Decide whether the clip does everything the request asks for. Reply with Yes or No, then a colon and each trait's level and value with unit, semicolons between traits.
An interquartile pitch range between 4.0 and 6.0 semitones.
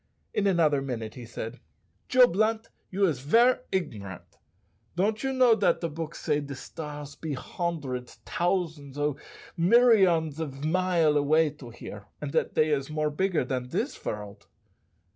Yes: average, 5.1 semitones